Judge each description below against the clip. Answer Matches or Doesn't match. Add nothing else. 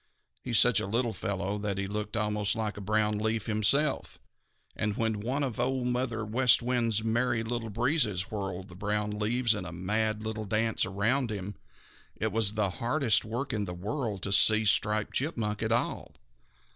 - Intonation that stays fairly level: Matches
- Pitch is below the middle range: Matches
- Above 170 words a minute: Matches